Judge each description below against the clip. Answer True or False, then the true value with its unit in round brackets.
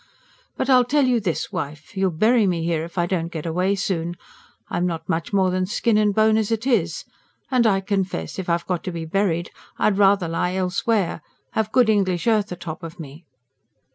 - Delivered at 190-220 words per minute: True (200 wpm)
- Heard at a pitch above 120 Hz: True (185 Hz)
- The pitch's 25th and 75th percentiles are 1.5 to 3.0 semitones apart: False (4.0 semitones)